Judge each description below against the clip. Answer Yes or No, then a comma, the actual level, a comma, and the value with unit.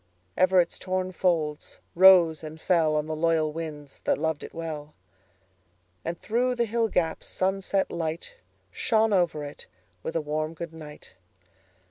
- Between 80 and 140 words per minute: Yes, slow, 135 wpm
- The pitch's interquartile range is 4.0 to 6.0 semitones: No, average, 3.6 semitones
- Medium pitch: Yes, medium, 160 Hz